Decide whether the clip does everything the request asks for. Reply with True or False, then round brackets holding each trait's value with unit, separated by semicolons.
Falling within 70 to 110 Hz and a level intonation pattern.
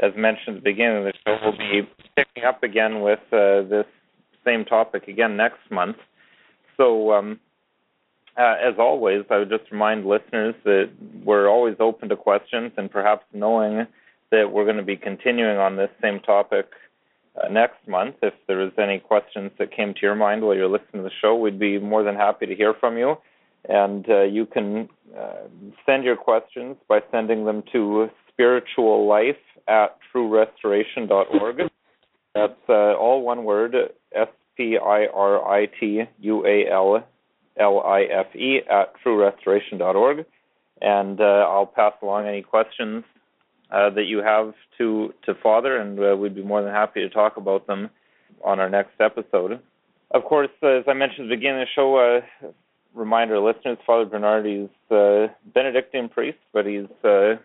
True (105 Hz; 2.1 semitones)